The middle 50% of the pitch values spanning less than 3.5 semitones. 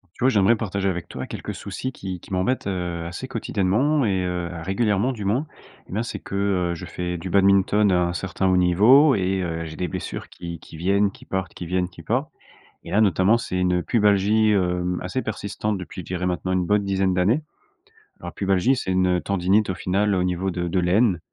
Yes: narrow, 2.6 semitones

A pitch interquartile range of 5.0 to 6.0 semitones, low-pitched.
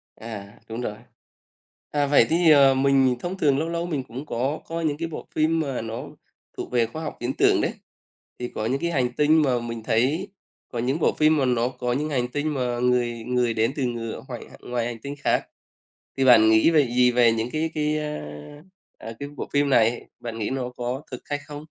No: average, 3.9 semitones; low, 130 Hz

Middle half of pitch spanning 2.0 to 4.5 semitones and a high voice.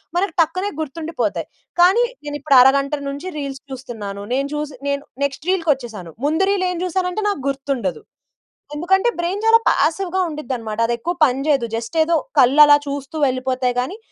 No: average, 5.1 semitones; very high, 285 Hz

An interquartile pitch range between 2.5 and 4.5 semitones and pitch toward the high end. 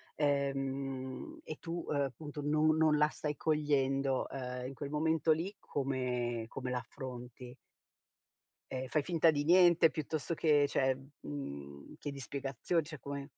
No: average, 2.8 semitones; medium, 140 Hz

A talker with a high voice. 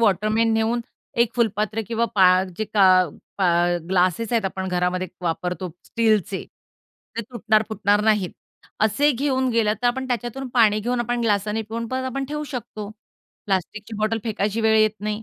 Yes: high, 215 Hz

